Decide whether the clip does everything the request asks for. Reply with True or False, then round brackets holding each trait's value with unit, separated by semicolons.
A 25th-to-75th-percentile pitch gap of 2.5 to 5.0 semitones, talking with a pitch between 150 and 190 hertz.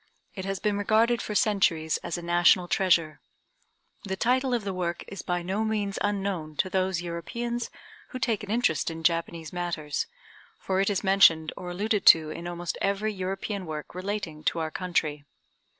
True (3.4 semitones; 185 Hz)